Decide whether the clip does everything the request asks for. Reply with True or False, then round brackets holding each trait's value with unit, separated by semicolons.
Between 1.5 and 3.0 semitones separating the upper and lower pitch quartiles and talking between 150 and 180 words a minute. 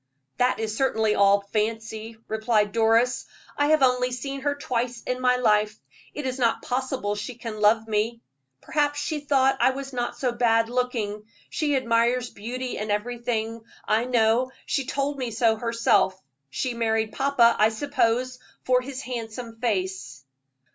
True (2.5 semitones; 155 wpm)